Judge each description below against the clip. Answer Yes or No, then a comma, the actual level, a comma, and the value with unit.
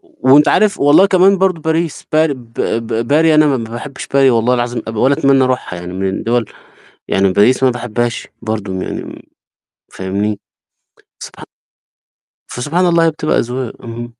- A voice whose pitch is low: Yes, low, 125 Hz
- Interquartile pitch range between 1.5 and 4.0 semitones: No, average, 5.2 semitones